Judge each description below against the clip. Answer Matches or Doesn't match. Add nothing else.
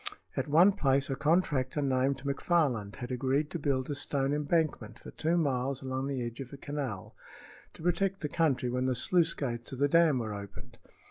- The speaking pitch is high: Doesn't match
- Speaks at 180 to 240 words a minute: Matches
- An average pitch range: Matches